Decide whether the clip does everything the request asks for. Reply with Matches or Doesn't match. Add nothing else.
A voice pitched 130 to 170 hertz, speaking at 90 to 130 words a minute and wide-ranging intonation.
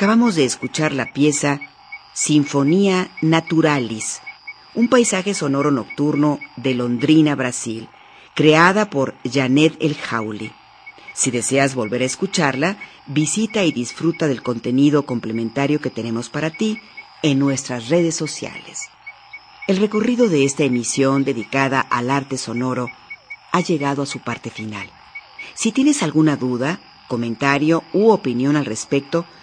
Doesn't match